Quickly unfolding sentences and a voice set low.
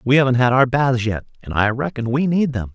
Yes: fast, 260 wpm; low, 125 Hz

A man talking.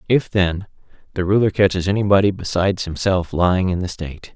Yes: male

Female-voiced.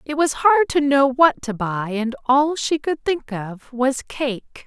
Yes: female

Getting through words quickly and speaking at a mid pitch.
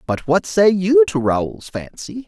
No: average, 185 wpm; medium, 165 Hz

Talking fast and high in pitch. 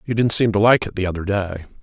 No: fast, 295 wpm; low, 100 Hz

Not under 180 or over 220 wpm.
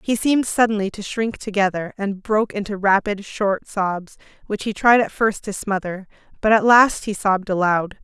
Yes: average, 185 wpm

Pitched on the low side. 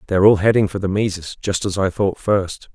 Yes: very low, 95 Hz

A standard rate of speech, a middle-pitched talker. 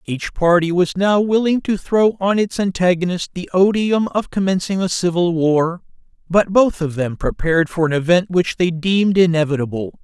Yes: average, 175 wpm; medium, 180 Hz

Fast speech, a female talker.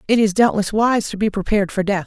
Yes: fast, 260 wpm; female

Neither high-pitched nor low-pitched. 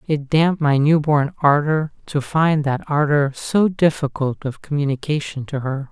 Yes: medium, 145 Hz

